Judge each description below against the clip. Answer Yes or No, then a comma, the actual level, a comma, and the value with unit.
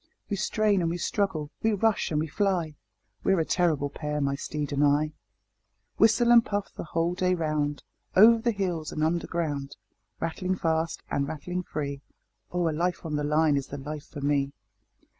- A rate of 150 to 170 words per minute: No, average, 185 wpm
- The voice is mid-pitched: Yes, medium, 160 Hz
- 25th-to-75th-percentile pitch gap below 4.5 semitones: Yes, average, 3.7 semitones